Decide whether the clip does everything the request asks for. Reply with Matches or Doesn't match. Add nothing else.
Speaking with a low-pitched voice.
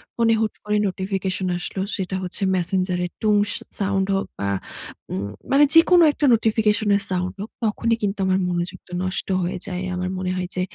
Doesn't match